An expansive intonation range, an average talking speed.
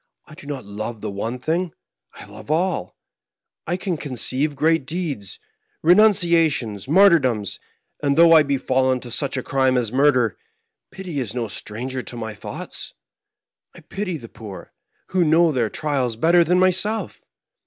Yes: wide, 5.9 semitones; average, 155 wpm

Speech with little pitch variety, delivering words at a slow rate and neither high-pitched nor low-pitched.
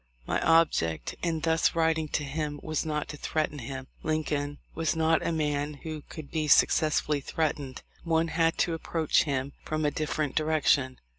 No: narrow, 1.8 semitones; average, 165 wpm; medium, 155 Hz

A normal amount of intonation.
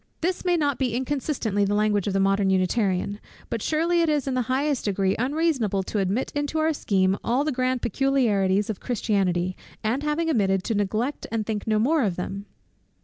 No: wide, 6.2 semitones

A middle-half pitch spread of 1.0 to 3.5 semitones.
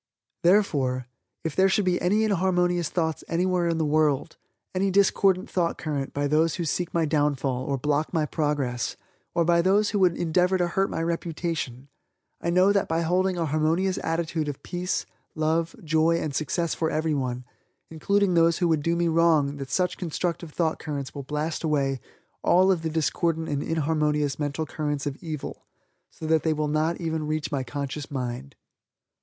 Yes: average, 2.9 semitones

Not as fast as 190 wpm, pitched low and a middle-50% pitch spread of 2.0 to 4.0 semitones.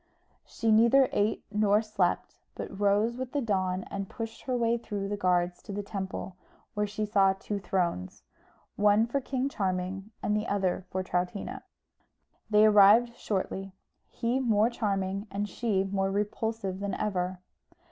No: average, 155 wpm; high, 205 Hz; narrow, 2.6 semitones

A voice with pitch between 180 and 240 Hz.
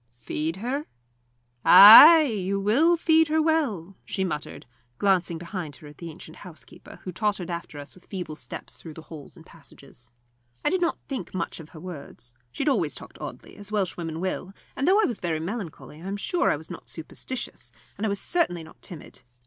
Yes: medium, 185 Hz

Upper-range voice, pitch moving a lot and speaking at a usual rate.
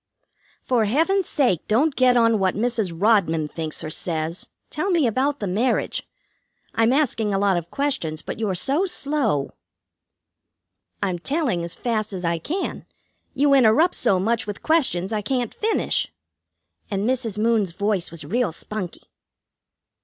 Yes: high, 220 Hz; wide, 6.5 semitones; average, 150 wpm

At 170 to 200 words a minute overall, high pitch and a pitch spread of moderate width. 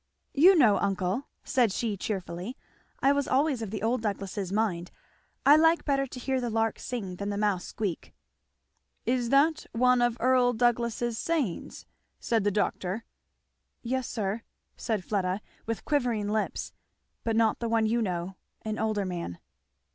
No: average, 155 wpm; high, 225 Hz; average, 3.8 semitones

